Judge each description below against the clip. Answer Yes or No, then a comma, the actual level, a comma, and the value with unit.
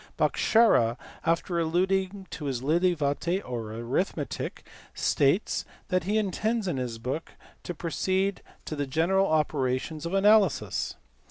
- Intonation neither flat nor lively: No, wide, 5.7 semitones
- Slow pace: Yes, slow, 120 wpm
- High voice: No, medium, 165 Hz